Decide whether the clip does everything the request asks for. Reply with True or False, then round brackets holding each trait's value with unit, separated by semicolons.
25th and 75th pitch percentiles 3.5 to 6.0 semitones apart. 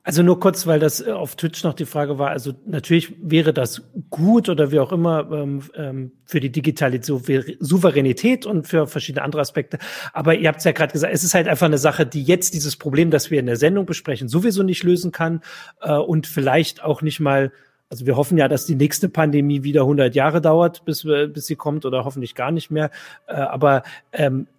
False (2.7 semitones)